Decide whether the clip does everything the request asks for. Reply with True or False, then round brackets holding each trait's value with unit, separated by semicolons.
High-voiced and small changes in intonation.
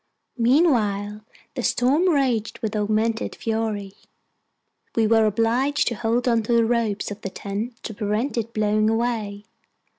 True (225 Hz; 2.3 semitones)